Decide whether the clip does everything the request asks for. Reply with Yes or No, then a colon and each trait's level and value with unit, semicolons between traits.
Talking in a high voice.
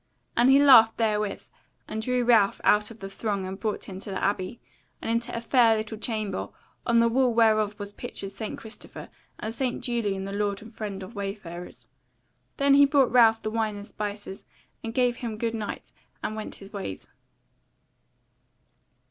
Yes: high, 220 Hz